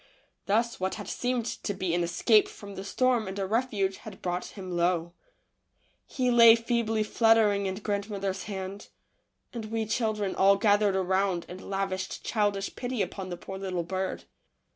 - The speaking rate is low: No, average, 165 wpm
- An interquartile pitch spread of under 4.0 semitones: Yes, average, 2.7 semitones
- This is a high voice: Yes, high, 200 Hz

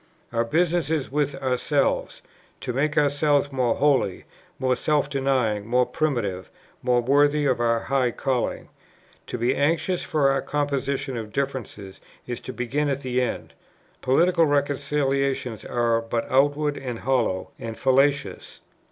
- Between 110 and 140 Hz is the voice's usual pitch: Yes, low, 135 Hz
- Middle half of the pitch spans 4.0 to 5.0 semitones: No, average, 2.9 semitones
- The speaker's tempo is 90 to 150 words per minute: Yes, average, 140 wpm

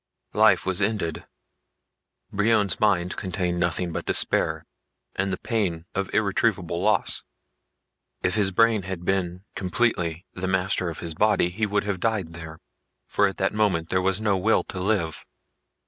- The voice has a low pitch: Yes, very low, 95 Hz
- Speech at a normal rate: Yes, average, 160 wpm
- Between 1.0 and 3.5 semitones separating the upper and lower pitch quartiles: Yes, average, 2.9 semitones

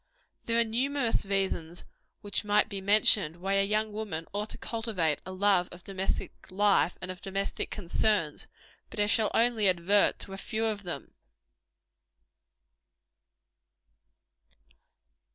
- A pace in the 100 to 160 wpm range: Yes, slow, 135 wpm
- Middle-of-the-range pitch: No, high, 200 Hz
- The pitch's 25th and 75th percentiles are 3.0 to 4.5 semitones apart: No, narrow, 2.6 semitones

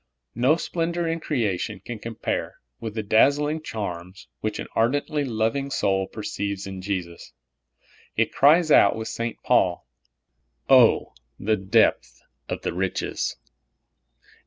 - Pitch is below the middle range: Yes, low, 110 Hz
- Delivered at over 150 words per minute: No, slow, 135 wpm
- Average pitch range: No, wide, 6.4 semitones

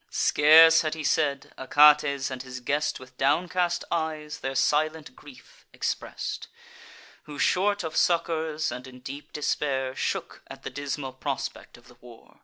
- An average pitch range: Yes, average, 3.1 semitones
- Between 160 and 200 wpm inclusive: No, average, 150 wpm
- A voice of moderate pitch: Yes, medium, 145 Hz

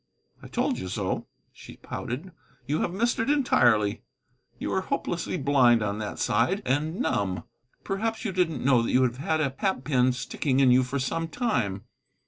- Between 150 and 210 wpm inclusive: Yes, average, 180 wpm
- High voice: No, low, 135 Hz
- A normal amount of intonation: No, wide, 7.0 semitones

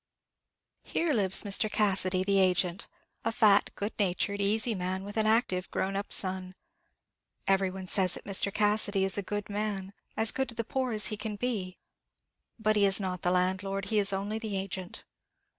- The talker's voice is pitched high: Yes, high, 200 Hz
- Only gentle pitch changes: Yes, narrow, 2.2 semitones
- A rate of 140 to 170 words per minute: No, average, 185 wpm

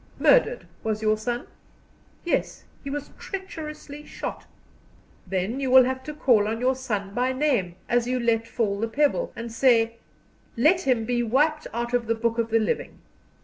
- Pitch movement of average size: Yes, average, 3.6 semitones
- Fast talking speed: No, average, 175 wpm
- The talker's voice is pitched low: No, high, 245 Hz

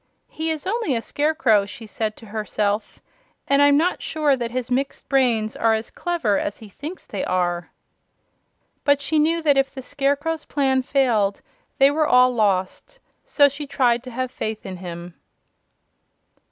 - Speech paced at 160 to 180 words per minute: Yes, average, 165 wpm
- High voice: Yes, very high, 255 Hz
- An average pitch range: Yes, average, 5.0 semitones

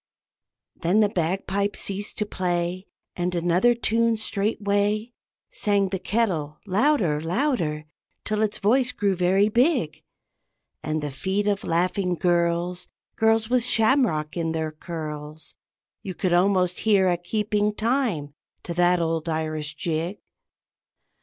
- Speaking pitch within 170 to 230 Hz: Yes, medium, 185 Hz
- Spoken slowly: Yes, slow, 125 wpm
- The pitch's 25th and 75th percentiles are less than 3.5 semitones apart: No, average, 4.1 semitones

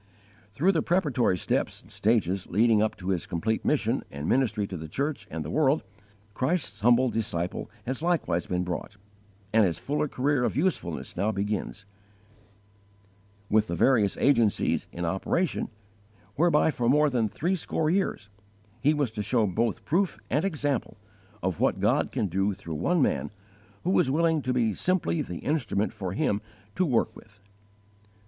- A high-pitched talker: No, low, 110 Hz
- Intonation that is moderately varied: No, wide, 7.2 semitones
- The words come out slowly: No, average, 160 wpm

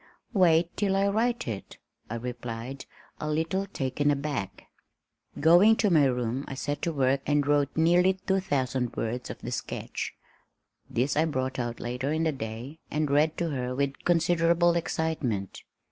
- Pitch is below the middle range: No, medium, 145 Hz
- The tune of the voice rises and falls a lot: No, average, 4.7 semitones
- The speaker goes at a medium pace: Yes, average, 160 wpm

